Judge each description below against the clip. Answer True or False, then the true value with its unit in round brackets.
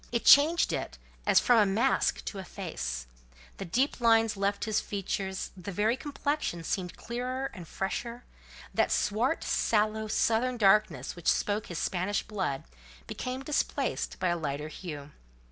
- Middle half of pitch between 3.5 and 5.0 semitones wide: True (4.5 semitones)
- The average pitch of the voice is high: True (210 Hz)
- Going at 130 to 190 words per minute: True (150 wpm)